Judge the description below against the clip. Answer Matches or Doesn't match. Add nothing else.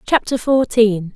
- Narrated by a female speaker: Matches